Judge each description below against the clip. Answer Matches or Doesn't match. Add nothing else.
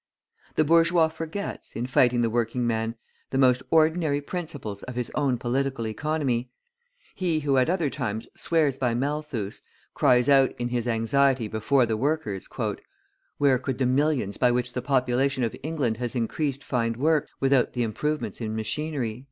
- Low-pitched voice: Matches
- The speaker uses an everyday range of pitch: Matches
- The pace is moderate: Matches